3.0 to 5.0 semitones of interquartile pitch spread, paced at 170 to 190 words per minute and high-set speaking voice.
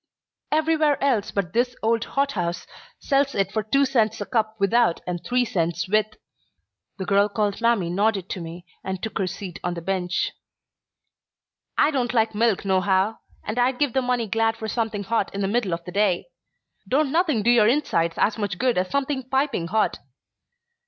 Yes: average, 4.5 semitones; average, 185 wpm; high, 220 Hz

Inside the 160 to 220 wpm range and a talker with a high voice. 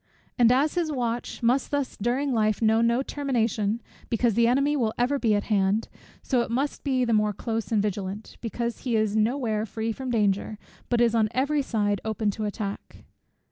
Yes: average, 195 wpm; high, 230 Hz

